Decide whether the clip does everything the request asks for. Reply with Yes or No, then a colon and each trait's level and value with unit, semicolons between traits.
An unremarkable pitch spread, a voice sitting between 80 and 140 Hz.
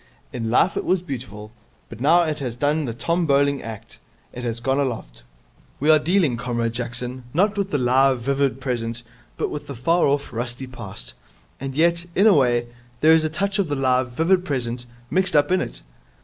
Yes: average, 4.7 semitones; low, 135 Hz